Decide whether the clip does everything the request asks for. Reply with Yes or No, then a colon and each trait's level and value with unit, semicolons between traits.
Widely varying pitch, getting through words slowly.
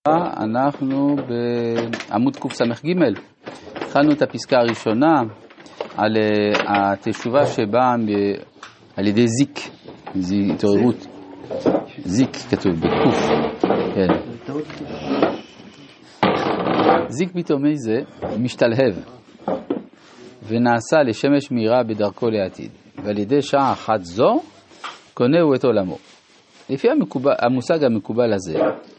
No: average, 4.2 semitones; slow, 85 wpm